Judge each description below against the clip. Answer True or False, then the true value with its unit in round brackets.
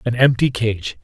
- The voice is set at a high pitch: False (120 Hz)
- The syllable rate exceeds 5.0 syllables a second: False (4.5 syllables/s)